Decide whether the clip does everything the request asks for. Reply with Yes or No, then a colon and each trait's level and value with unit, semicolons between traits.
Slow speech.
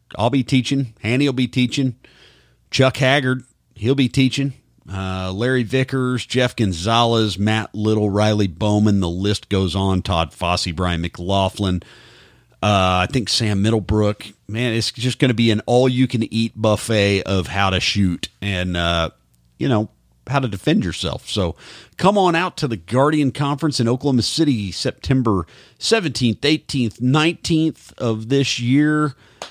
No: average, 145 wpm